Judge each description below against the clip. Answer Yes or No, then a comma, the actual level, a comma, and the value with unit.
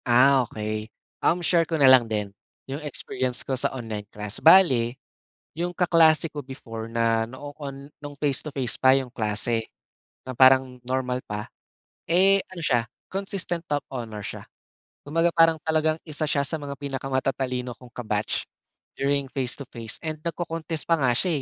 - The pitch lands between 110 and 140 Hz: Yes, low, 135 Hz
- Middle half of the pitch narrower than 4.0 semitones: No, average, 4.6 semitones